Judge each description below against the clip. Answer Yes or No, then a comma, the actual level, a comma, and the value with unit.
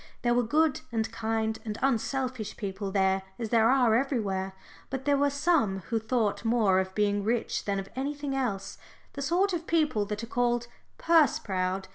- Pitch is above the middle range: Yes, high, 230 Hz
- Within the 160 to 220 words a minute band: Yes, average, 180 wpm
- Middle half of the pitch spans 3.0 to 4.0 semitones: No, average, 4.8 semitones